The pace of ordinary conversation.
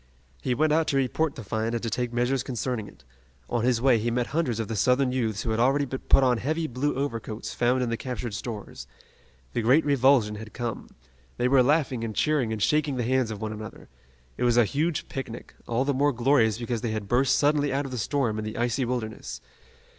No: fast, 225 wpm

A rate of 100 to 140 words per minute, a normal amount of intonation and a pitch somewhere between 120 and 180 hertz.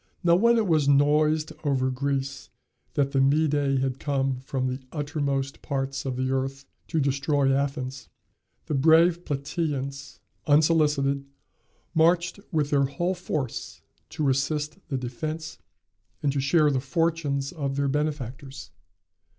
No: slow, 135 wpm; narrow, 2.3 semitones; medium, 140 Hz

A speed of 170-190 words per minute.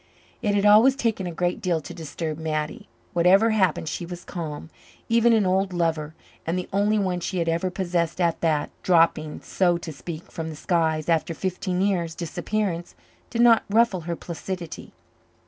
Yes: average, 175 wpm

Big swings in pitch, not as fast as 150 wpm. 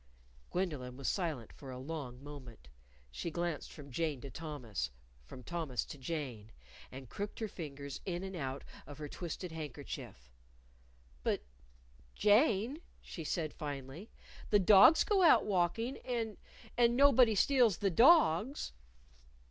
Yes: wide, 7.1 semitones; average, 140 wpm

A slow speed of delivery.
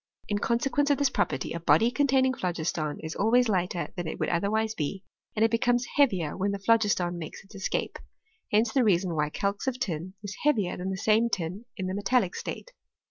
No: average, 200 wpm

